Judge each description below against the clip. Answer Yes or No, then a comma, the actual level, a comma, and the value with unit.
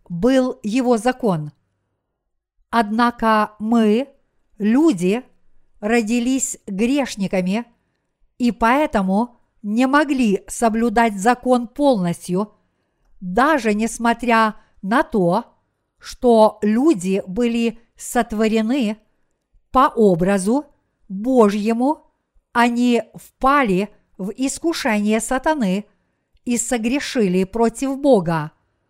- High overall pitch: Yes, high, 230 Hz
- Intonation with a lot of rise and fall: No, average, 3.7 semitones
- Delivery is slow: Yes, slow, 75 wpm